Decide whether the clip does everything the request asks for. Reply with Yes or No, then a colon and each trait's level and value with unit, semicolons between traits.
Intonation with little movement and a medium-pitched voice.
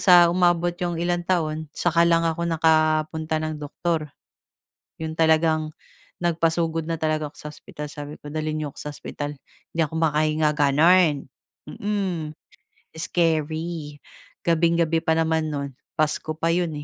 Yes: narrow, 1.6 semitones; medium, 160 Hz